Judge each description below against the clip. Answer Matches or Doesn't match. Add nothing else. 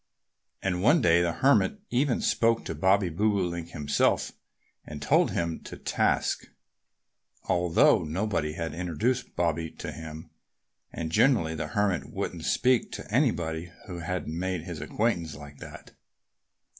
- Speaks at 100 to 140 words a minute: Matches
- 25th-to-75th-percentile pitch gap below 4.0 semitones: Doesn't match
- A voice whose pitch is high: Doesn't match